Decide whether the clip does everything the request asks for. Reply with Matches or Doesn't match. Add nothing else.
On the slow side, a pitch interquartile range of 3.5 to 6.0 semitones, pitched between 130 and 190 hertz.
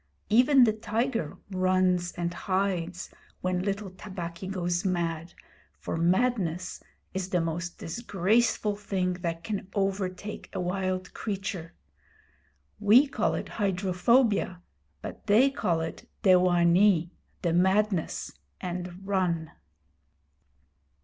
Doesn't match